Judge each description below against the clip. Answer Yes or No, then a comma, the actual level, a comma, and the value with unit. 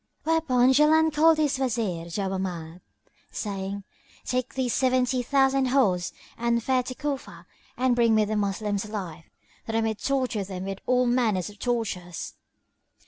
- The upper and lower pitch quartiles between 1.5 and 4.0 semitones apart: No, average, 4.9 semitones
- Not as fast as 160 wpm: Yes, average, 145 wpm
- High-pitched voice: Yes, high, 235 Hz